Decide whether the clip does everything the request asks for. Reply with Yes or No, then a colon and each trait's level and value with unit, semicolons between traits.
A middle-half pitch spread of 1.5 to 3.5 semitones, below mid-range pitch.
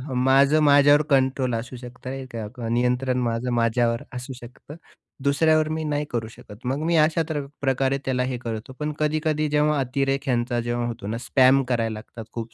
Yes: average, 3.2 semitones; low, 130 Hz